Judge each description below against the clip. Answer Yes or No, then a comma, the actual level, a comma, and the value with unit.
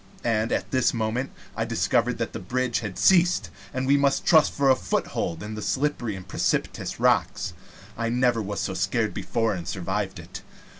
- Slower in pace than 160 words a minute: No, average, 185 wpm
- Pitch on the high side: No, low, 115 Hz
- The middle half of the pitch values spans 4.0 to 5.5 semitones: Yes, average, 4.7 semitones